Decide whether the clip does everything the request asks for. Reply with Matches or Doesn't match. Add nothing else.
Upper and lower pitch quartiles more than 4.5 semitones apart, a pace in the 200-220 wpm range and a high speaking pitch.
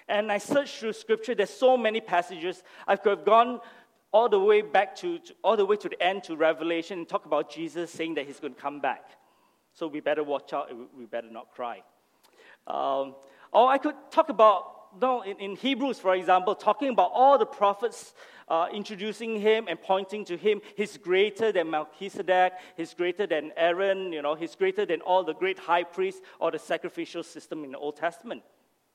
Matches